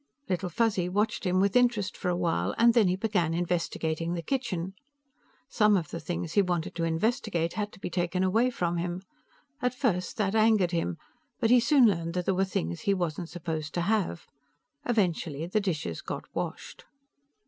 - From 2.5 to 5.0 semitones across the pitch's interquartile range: Yes, average, 4.0 semitones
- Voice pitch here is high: No, medium, 180 Hz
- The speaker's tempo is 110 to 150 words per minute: No, average, 185 wpm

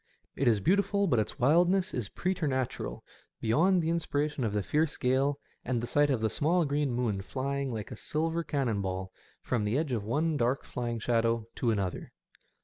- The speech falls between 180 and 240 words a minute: Yes, average, 185 wpm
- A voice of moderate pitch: No, low, 130 Hz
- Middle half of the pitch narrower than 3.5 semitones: No, average, 5.1 semitones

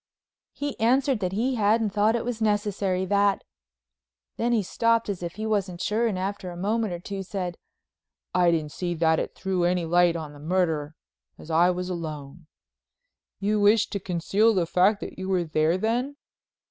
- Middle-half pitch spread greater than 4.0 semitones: No, average, 3.7 semitones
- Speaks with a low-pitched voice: No, high, 190 Hz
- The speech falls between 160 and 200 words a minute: Yes, average, 180 wpm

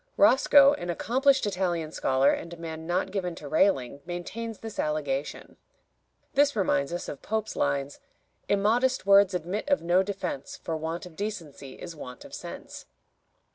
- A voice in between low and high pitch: Yes, medium, 180 Hz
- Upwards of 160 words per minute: No, average, 155 wpm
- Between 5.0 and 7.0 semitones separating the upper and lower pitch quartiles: Yes, average, 5.3 semitones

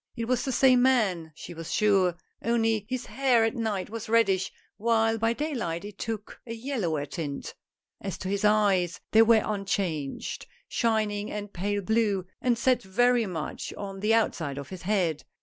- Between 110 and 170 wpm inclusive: No, average, 185 wpm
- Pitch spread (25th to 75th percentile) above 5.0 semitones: No, average, 3.5 semitones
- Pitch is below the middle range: No, high, 210 Hz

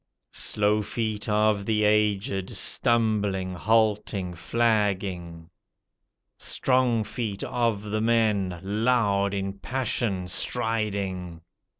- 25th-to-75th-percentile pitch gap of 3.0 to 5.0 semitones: No, narrow, 2.5 semitones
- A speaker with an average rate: No, slow, 85 wpm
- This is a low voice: Yes, low, 105 Hz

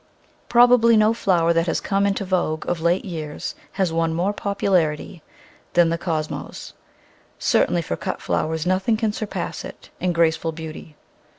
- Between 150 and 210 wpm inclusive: Yes, average, 160 wpm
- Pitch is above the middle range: No, medium, 175 Hz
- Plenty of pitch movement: No, average, 3.5 semitones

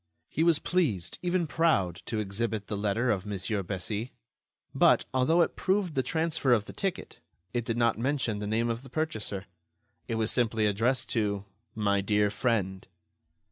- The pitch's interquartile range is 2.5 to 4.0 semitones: No, average, 4.8 semitones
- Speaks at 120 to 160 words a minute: No, average, 170 wpm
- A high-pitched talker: No, low, 115 Hz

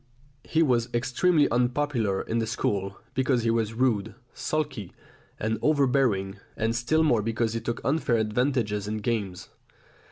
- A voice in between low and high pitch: No, low, 115 Hz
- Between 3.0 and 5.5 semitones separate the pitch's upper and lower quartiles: Yes, average, 3.4 semitones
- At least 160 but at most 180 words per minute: No, average, 140 wpm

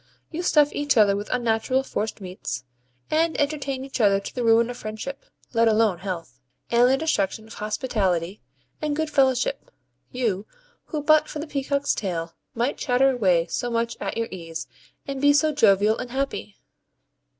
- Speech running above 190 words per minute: No, average, 170 wpm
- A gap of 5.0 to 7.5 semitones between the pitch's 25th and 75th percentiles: Yes, wide, 5.5 semitones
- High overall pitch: Yes, high, 240 Hz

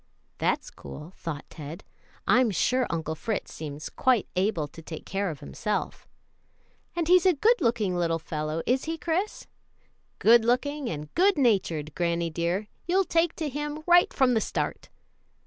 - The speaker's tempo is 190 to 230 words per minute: No, average, 160 wpm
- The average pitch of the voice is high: Yes, high, 215 Hz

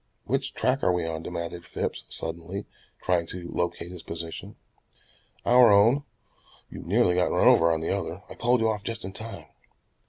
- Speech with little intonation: No, average, 4.5 semitones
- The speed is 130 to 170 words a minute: No, average, 180 wpm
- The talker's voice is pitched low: Yes, very low, 90 Hz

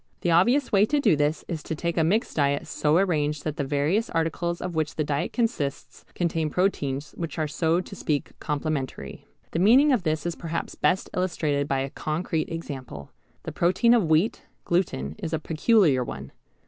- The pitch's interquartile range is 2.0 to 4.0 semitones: Yes, average, 3.6 semitones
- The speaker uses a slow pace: No, average, 185 wpm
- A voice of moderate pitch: Yes, medium, 160 Hz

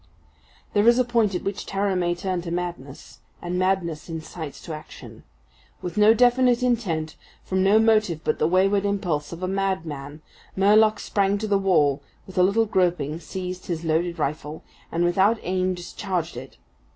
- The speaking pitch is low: No, medium, 185 Hz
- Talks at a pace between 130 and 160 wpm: No, average, 170 wpm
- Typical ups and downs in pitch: Yes, average, 3.4 semitones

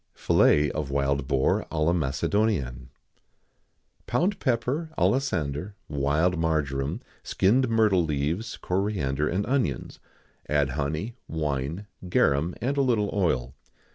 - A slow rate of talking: Yes, slow, 120 wpm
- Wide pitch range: Yes, wide, 7.2 semitones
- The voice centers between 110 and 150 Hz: No, very low, 80 Hz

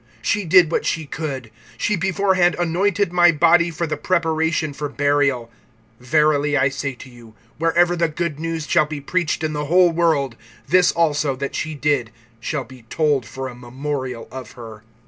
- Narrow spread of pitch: No, average, 3.9 semitones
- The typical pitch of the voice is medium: Yes, medium, 150 Hz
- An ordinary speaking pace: Yes, average, 175 wpm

